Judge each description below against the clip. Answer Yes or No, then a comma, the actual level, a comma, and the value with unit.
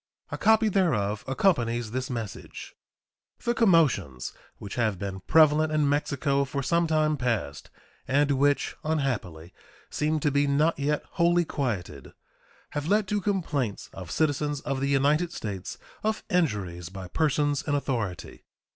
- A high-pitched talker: No, medium, 140 Hz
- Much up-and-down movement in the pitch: Yes, wide, 5.9 semitones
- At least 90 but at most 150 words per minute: Yes, average, 140 wpm